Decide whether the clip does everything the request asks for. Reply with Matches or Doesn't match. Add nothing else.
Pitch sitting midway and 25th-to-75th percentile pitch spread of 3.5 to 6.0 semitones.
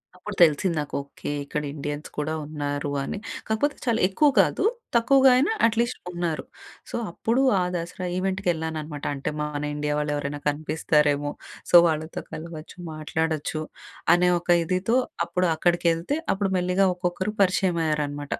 Matches